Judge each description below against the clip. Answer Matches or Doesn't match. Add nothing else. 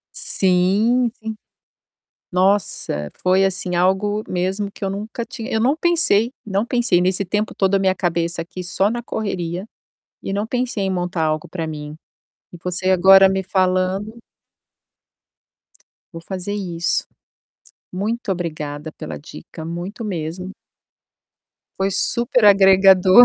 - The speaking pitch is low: Doesn't match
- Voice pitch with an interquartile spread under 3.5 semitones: Matches